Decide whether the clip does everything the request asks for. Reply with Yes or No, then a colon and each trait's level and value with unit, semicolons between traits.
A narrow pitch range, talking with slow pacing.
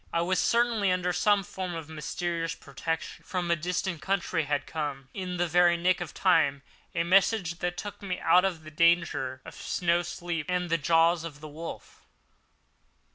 No: narrow, 2.1 semitones; average, 185 wpm